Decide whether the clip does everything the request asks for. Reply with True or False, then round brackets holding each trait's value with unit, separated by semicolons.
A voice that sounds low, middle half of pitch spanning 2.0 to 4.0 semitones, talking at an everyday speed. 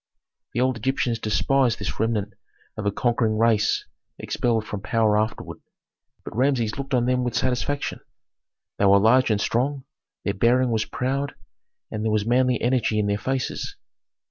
True (115 Hz; 3.1 semitones; 160 wpm)